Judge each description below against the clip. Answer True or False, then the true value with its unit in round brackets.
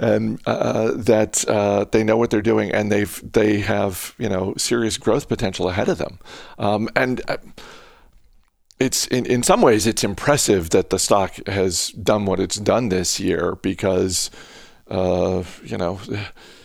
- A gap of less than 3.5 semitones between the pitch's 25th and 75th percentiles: True (2.9 semitones)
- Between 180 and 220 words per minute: False (160 wpm)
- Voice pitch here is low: True (105 Hz)